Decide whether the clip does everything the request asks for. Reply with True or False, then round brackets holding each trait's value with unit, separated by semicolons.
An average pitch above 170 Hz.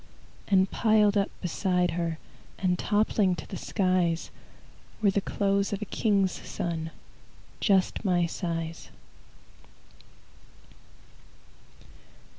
True (190 Hz)